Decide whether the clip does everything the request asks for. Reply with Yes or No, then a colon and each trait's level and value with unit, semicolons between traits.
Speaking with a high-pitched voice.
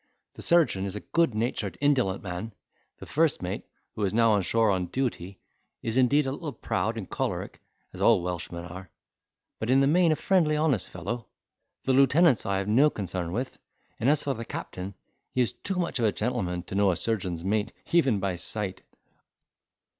No: low, 110 Hz